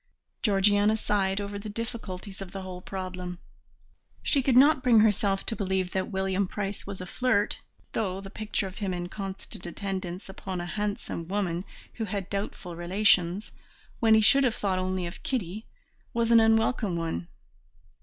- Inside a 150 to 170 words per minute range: Yes, average, 165 wpm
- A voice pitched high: Yes, high, 195 Hz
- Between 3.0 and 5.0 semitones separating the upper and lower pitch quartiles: No, narrow, 2.6 semitones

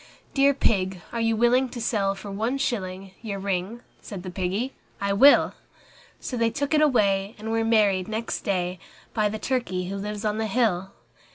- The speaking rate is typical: Yes, average, 190 wpm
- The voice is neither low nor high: No, high, 210 Hz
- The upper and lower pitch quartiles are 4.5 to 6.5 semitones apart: No, average, 3.4 semitones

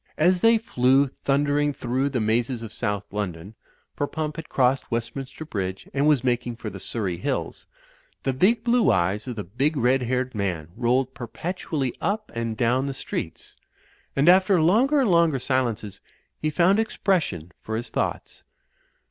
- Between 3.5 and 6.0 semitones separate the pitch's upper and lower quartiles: Yes, wide, 5.5 semitones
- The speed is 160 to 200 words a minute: Yes, average, 165 wpm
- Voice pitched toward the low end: Yes, low, 130 Hz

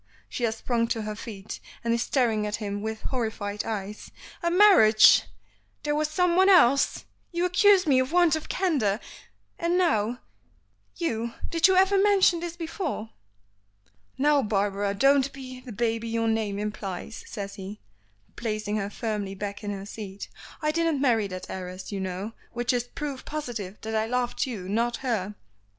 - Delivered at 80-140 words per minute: No, average, 165 wpm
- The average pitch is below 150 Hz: No, high, 230 Hz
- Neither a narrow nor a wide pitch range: No, wide, 6.2 semitones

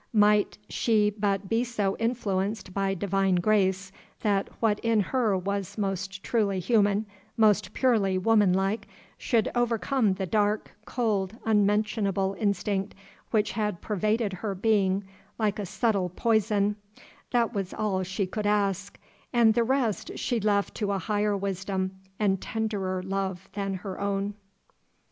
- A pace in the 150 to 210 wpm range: No, average, 140 wpm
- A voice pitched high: Yes, high, 205 Hz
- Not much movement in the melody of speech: Yes, narrow, 2.1 semitones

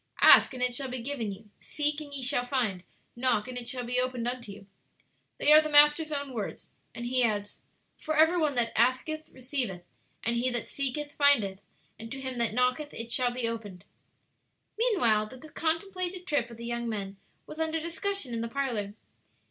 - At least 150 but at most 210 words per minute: Yes, average, 195 wpm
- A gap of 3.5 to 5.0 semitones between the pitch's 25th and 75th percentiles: Yes, average, 4.2 semitones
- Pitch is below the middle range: No, very high, 255 Hz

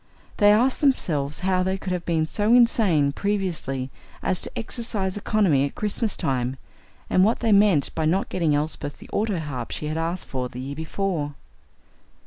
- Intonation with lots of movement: Yes, wide, 5.9 semitones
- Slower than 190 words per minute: Yes, average, 170 wpm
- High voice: No, medium, 180 Hz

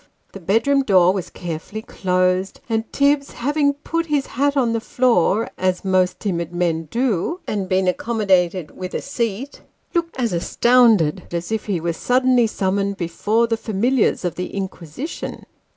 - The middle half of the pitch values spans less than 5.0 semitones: No, wide, 5.5 semitones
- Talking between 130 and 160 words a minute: Yes, average, 155 wpm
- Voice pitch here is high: Yes, high, 205 Hz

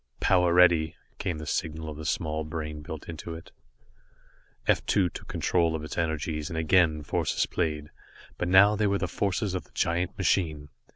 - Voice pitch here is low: Yes, very low, 80 Hz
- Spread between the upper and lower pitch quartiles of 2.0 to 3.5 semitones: Yes, narrow, 2.6 semitones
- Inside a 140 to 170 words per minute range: No, average, 180 wpm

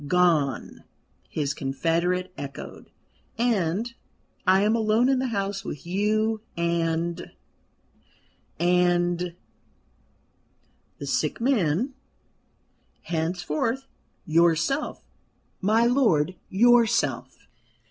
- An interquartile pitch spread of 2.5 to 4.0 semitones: No, average, 5.1 semitones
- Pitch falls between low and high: Yes, medium, 180 Hz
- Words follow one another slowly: Yes, slow, 80 wpm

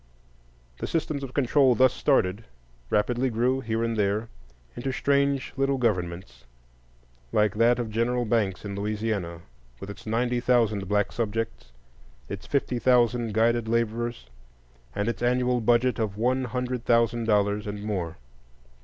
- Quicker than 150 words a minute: No, average, 140 wpm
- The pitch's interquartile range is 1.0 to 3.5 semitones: Yes, average, 3.0 semitones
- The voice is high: No, low, 115 Hz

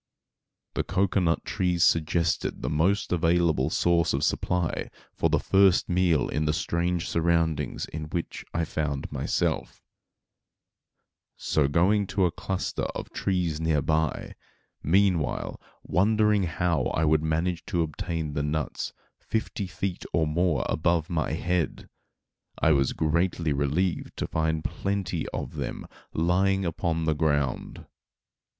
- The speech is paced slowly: Yes, slow, 130 wpm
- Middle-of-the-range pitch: No, very low, 85 Hz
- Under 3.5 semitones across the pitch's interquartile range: Yes, narrow, 2.6 semitones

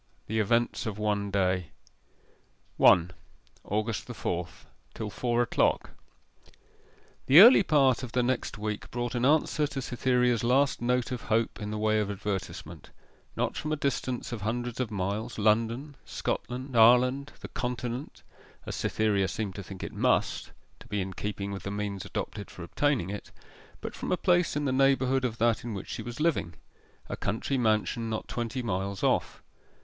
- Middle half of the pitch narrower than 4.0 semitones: Yes, average, 3.6 semitones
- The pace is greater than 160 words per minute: Yes, average, 175 wpm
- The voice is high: No, low, 115 Hz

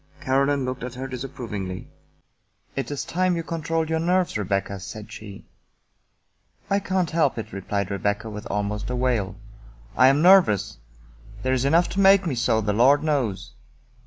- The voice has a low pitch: Yes, low, 130 Hz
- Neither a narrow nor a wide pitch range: No, wide, 7.4 semitones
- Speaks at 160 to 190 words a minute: Yes, average, 170 wpm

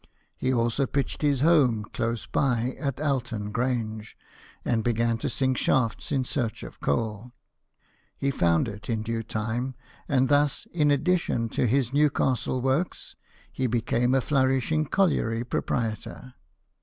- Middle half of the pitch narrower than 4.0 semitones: Yes, average, 3.3 semitones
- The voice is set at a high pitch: No, low, 125 Hz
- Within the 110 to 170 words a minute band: Yes, average, 145 wpm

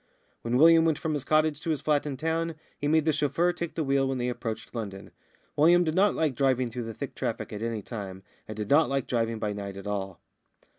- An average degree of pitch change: No, wide, 5.8 semitones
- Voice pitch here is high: No, low, 135 Hz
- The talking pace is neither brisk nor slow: No, fast, 235 wpm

